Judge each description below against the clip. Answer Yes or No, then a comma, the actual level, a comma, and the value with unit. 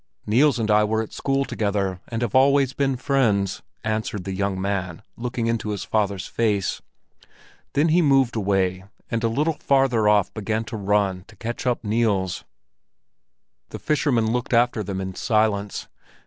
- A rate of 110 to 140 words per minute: No, average, 160 wpm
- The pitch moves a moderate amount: Yes, average, 3.5 semitones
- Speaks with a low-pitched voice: Yes, low, 110 Hz